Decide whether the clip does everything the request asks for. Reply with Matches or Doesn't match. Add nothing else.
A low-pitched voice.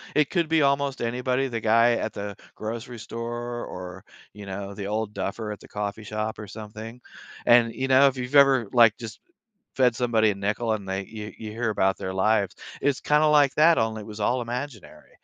Matches